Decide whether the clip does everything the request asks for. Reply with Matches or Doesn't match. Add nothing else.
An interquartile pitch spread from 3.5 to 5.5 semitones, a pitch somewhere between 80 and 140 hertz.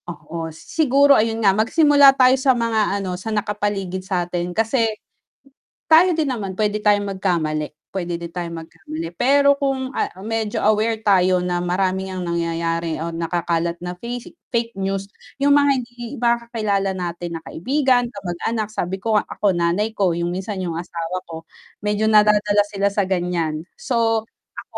Doesn't match